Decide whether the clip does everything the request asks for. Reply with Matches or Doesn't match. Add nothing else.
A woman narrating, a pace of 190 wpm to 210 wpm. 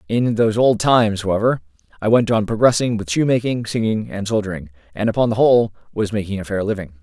Doesn't match